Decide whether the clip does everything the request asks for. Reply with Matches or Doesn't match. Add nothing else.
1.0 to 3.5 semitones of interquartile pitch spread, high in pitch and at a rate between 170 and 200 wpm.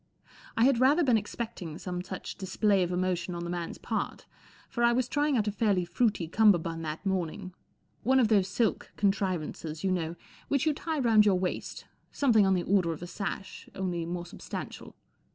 Doesn't match